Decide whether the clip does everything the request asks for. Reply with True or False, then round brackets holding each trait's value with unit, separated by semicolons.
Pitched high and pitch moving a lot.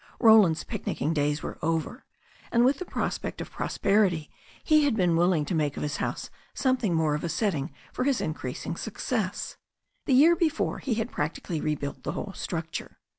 False (175 Hz; 7.4 semitones)